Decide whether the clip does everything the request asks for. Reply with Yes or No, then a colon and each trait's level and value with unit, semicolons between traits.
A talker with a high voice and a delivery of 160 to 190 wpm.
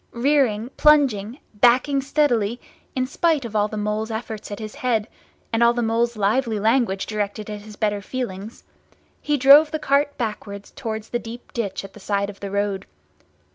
Yes: high, 225 Hz; average, 175 wpm